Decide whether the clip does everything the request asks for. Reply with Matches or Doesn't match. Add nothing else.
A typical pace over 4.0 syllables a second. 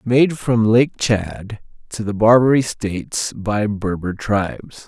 Doesn't match